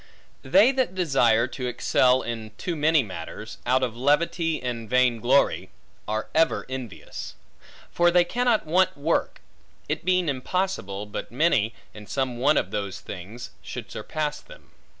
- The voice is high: No, low, 130 Hz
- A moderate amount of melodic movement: No, wide, 6.3 semitones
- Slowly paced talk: No, average, 150 wpm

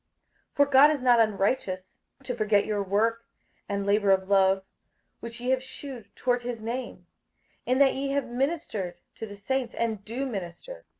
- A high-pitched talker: Yes, high, 230 Hz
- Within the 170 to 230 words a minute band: Yes, average, 175 wpm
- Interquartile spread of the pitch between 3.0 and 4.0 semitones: No, average, 4.5 semitones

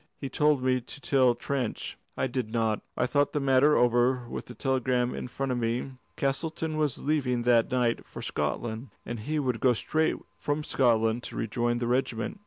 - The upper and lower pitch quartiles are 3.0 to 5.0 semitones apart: No, narrow, 2.6 semitones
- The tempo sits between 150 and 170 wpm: No, average, 190 wpm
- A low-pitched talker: Yes, low, 125 Hz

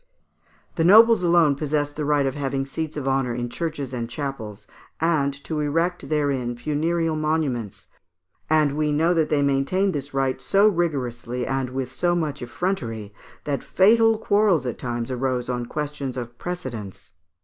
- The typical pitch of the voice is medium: Yes, medium, 145 Hz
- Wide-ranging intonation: No, average, 4.2 semitones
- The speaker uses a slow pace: No, average, 170 wpm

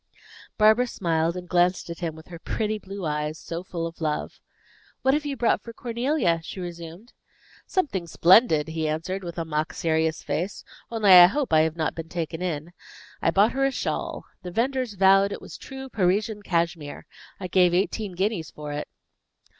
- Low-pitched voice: No, medium, 180 Hz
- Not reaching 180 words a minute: No, average, 185 wpm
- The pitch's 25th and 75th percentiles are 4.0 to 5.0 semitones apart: Yes, average, 4.7 semitones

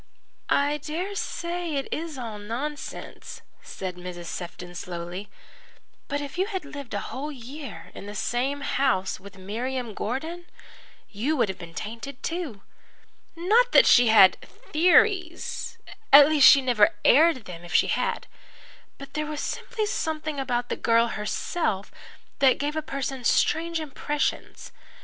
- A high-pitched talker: Yes, very high, 275 Hz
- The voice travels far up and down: Yes, wide, 6.6 semitones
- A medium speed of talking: Yes, average, 145 wpm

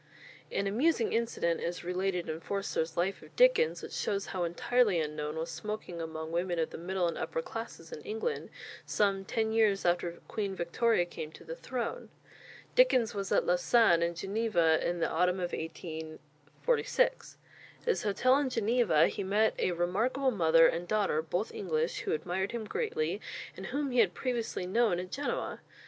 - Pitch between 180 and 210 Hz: Yes, high, 190 Hz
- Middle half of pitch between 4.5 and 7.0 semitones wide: Yes, wide, 5.5 semitones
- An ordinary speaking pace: Yes, average, 170 wpm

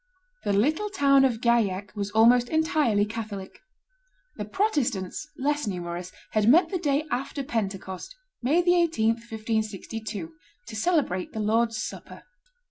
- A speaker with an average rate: No, slow, 125 wpm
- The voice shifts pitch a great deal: Yes, wide, 5.8 semitones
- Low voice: No, high, 225 Hz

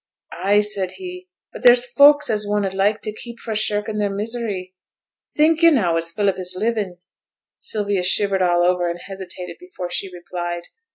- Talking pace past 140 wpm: Yes, average, 175 wpm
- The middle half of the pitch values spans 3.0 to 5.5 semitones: Yes, average, 3.9 semitones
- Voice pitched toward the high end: Yes, high, 205 Hz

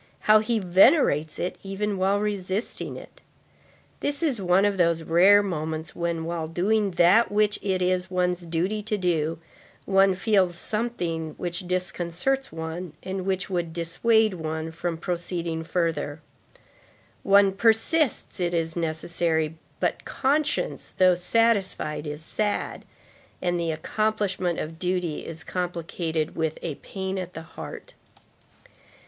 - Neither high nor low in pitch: Yes, medium, 180 Hz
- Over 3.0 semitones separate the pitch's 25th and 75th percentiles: Yes, average, 3.5 semitones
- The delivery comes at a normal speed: No, slow, 130 wpm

